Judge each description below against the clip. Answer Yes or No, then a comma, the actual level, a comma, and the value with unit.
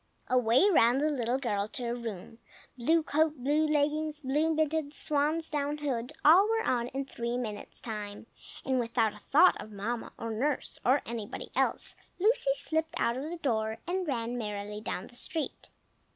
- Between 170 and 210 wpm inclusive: Yes, average, 175 wpm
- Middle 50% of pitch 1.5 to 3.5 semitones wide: No, average, 4.9 semitones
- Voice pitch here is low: No, very high, 265 Hz